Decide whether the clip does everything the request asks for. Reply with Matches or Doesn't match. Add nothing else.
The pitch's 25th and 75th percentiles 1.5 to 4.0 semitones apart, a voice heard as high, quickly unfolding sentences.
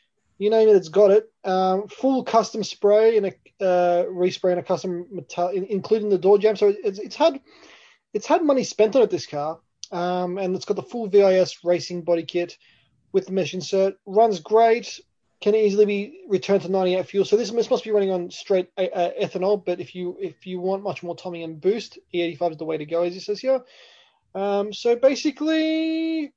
Matches